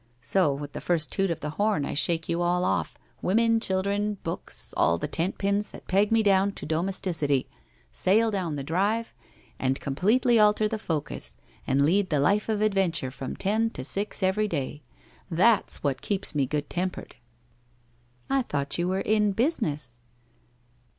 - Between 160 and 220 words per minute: Yes, average, 185 wpm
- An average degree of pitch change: No, wide, 6.1 semitones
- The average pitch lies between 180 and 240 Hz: Yes, medium, 185 Hz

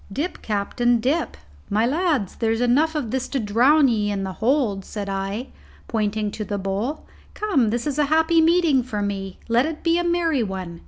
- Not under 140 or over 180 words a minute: No, average, 195 wpm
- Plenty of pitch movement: Yes, wide, 6.7 semitones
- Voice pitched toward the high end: Yes, high, 240 Hz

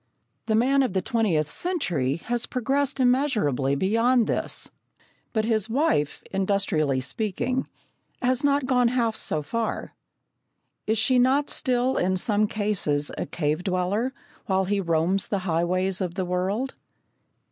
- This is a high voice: Yes, high, 210 Hz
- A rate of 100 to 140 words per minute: Yes, slow, 135 wpm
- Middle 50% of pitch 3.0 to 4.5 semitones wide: No, wide, 5.6 semitones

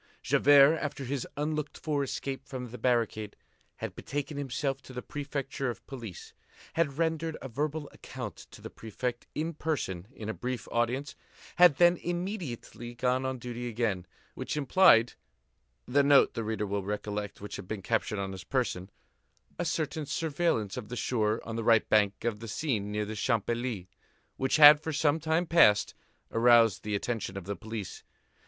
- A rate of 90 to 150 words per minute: No, average, 170 wpm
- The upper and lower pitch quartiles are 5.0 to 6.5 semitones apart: Yes, average, 5.3 semitones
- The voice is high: No, low, 125 Hz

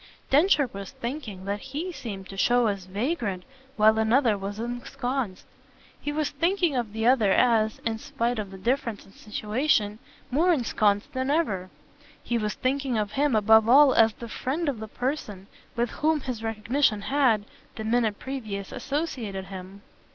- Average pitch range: Yes, average, 4.6 semitones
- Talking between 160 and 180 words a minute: Yes, average, 165 wpm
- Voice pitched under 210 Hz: No, high, 230 Hz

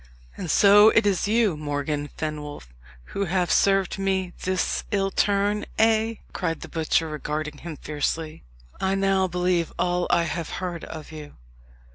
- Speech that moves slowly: No, average, 150 wpm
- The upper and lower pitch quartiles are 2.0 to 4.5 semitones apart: Yes, average, 4.0 semitones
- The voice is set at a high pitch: No, medium, 180 Hz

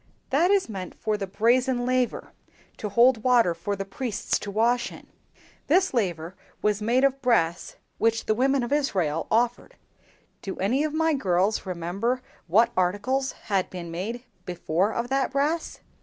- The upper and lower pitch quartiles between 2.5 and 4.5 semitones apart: No, average, 5.2 semitones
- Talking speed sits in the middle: Yes, average, 160 wpm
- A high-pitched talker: Yes, high, 230 Hz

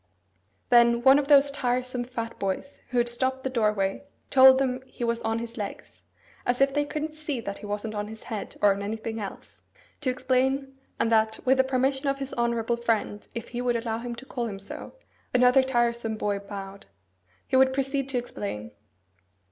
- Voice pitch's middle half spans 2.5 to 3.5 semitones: Yes, average, 3.0 semitones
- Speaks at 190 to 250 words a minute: Yes, average, 195 wpm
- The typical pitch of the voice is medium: No, high, 240 Hz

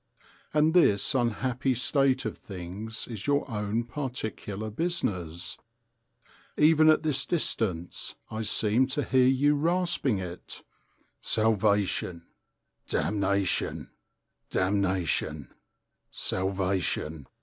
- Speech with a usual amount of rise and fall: No, wide, 5.9 semitones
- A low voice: Yes, low, 110 Hz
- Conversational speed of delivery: No, slow, 90 wpm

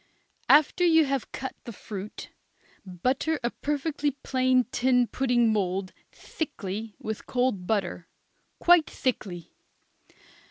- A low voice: No, very high, 250 Hz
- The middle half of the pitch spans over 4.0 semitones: Yes, average, 5.3 semitones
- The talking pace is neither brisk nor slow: No, slow, 110 wpm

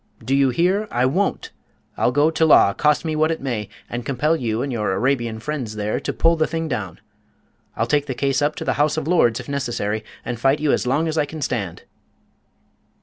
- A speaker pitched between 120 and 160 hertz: Yes, medium, 140 Hz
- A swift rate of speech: Yes, fast, 220 wpm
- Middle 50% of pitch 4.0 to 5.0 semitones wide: Yes, average, 4.7 semitones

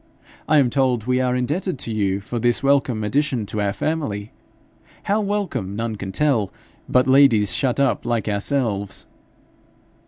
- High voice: No, low, 125 Hz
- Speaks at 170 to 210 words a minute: No, average, 155 wpm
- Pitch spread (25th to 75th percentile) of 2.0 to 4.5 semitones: No, average, 4.9 semitones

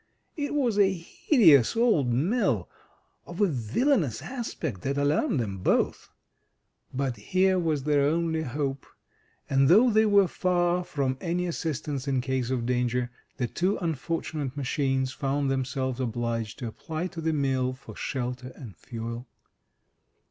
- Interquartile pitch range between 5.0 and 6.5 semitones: Yes, wide, 5.5 semitones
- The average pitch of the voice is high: No, medium, 140 Hz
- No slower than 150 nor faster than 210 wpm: No, average, 140 wpm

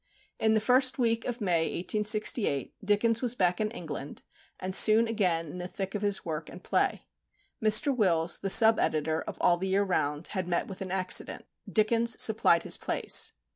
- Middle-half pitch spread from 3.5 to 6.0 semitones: Yes, average, 4.2 semitones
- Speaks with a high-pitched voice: Yes, high, 200 Hz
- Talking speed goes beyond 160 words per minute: Yes, average, 185 wpm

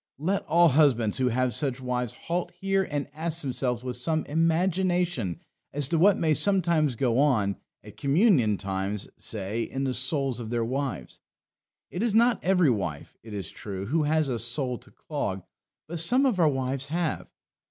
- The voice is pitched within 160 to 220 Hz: No, medium, 140 Hz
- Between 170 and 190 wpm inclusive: Yes, average, 175 wpm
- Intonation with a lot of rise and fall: Yes, wide, 5.9 semitones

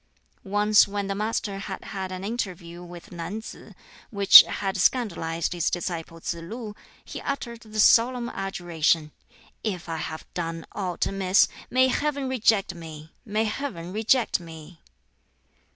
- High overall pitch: Yes, high, 195 Hz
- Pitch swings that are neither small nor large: Yes, average, 4.5 semitones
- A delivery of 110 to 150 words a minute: Yes, average, 140 wpm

